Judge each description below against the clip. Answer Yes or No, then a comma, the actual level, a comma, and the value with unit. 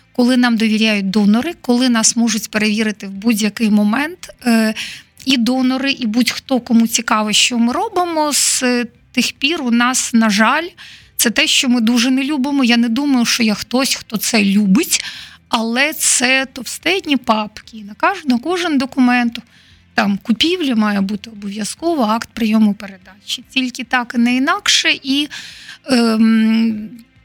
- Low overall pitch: No, high, 240 Hz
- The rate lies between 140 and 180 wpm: Yes, average, 145 wpm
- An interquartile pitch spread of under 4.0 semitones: Yes, average, 3.3 semitones